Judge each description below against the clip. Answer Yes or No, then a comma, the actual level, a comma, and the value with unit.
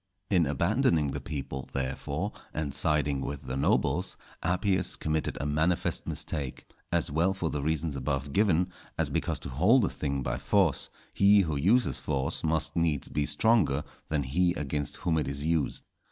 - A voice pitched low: Yes, very low, 75 Hz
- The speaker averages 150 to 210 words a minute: Yes, average, 170 wpm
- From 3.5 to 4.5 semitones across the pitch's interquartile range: Yes, average, 4.2 semitones